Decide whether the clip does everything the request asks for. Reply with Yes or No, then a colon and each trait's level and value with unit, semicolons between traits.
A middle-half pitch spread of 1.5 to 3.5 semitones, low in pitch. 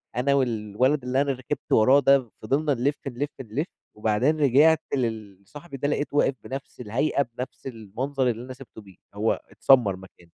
No: average, 4.2 semitones; low, 130 Hz